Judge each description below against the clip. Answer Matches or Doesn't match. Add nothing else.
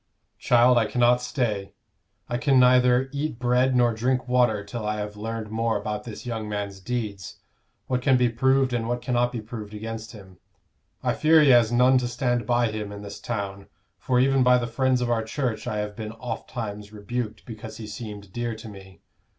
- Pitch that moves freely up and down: Doesn't match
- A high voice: Doesn't match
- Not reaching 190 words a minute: Doesn't match